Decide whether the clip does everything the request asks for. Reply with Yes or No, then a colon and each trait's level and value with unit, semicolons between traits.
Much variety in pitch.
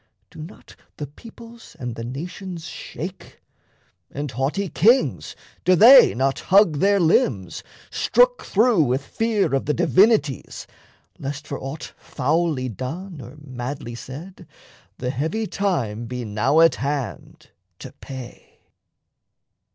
Yes: wide, 6.9 semitones